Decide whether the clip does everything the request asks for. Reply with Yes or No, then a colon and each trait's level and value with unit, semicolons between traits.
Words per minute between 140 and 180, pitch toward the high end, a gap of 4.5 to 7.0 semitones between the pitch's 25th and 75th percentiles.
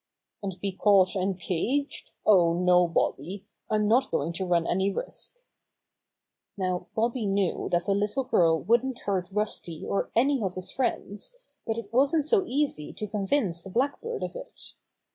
Yes: average, 160 wpm; high, 200 Hz; wide, 5.5 semitones